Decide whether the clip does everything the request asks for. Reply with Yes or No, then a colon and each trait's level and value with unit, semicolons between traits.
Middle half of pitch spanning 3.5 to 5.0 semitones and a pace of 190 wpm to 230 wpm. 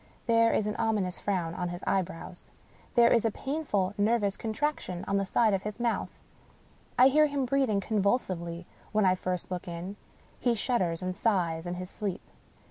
No: average, 4.2 semitones; average, 180 wpm